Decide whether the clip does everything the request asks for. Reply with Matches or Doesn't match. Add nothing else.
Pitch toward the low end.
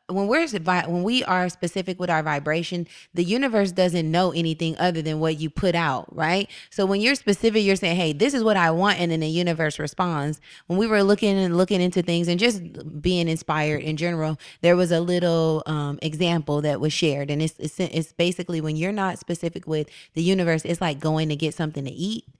Doesn't match